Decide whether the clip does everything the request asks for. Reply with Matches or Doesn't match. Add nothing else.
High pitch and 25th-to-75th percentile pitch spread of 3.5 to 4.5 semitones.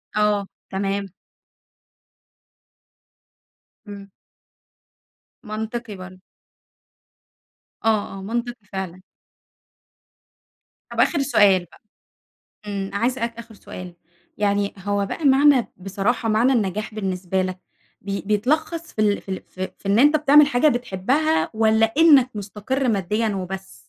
Matches